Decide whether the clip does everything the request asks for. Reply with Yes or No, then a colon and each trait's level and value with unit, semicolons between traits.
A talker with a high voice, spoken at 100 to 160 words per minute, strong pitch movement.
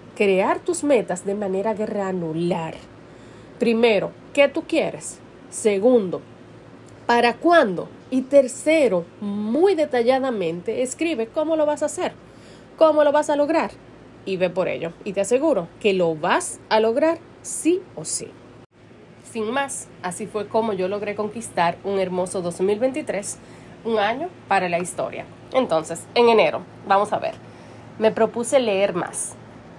Yes: high, 220 Hz; average, 140 wpm; wide, 6.5 semitones